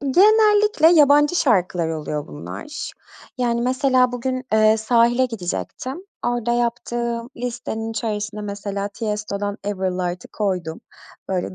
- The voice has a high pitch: Yes, high, 230 Hz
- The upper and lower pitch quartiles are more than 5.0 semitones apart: No, average, 4.1 semitones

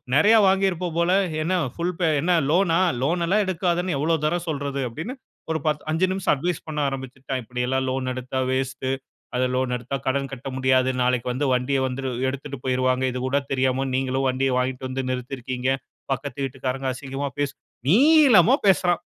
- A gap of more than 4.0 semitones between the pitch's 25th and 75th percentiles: Yes, average, 4.7 semitones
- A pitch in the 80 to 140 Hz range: Yes, low, 135 Hz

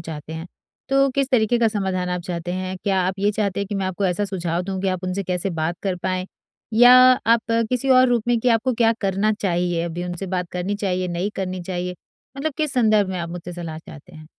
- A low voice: No, high, 190 Hz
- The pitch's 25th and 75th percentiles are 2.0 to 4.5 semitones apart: Yes, average, 3.5 semitones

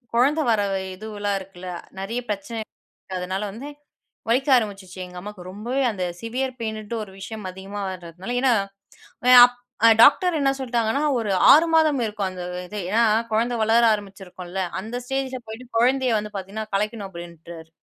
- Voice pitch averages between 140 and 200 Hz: No, high, 215 Hz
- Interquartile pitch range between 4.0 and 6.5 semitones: Yes, average, 4.3 semitones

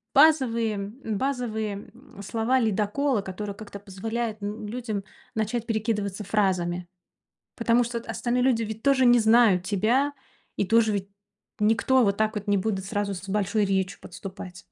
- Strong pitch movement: No, average, 2.8 semitones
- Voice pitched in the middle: No, high, 215 Hz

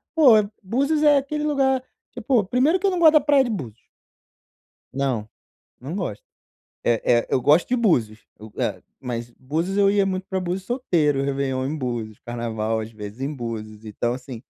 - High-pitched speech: No, medium, 150 Hz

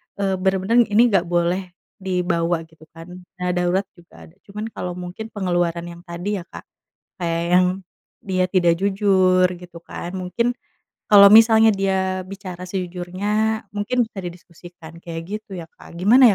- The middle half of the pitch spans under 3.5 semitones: Yes, narrow, 2.4 semitones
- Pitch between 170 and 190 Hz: Yes, medium, 185 Hz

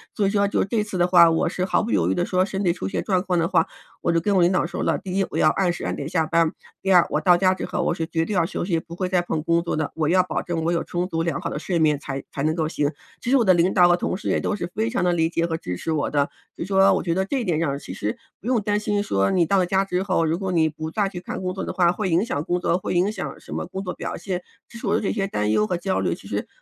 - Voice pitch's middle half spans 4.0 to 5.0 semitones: No, average, 2.7 semitones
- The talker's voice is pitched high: No, medium, 175 Hz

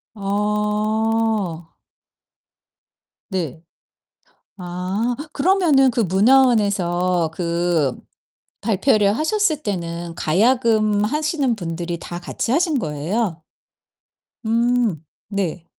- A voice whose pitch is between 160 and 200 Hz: No, high, 210 Hz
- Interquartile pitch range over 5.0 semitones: Yes, wide, 5.4 semitones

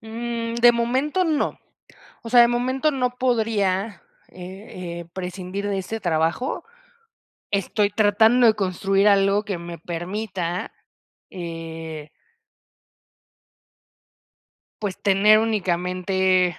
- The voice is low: No, high, 200 Hz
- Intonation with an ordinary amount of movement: Yes, average, 4.1 semitones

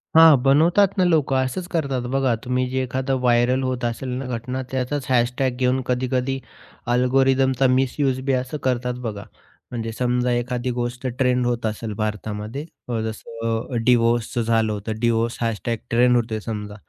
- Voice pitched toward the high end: No, low, 125 Hz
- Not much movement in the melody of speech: Yes, narrow, 2.2 semitones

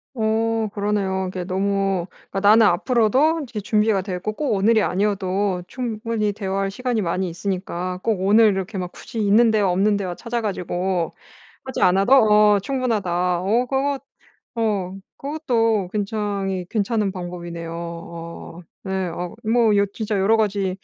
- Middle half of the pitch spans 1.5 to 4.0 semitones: Yes, average, 3.2 semitones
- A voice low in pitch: No, high, 200 Hz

